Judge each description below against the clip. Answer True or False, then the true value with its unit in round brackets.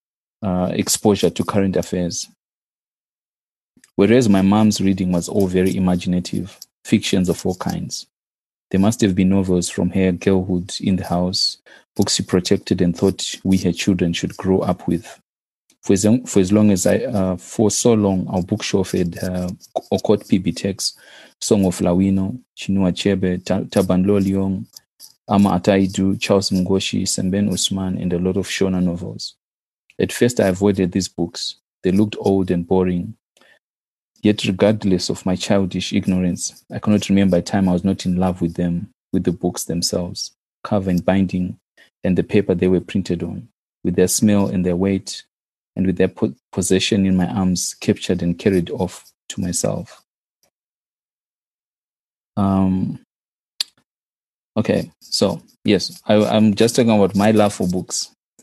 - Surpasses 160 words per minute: False (155 wpm)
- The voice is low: True (95 Hz)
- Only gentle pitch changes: True (1.8 semitones)